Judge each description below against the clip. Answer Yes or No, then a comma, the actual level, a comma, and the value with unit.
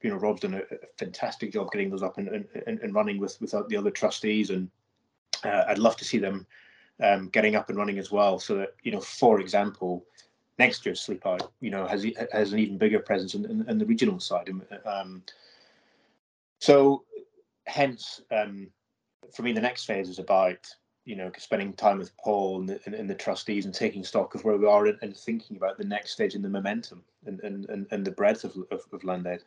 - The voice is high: No, low, 110 Hz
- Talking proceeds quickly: Yes, fast, 215 wpm